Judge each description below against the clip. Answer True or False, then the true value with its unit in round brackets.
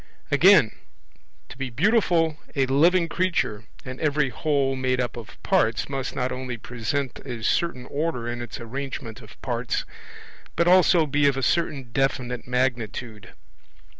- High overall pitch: False (135 Hz)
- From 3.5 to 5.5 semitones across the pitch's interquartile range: True (3.9 semitones)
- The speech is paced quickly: False (145 wpm)